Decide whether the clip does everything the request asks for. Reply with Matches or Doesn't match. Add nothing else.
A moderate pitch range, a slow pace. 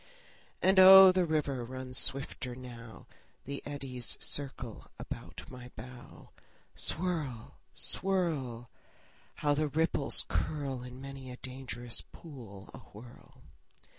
Matches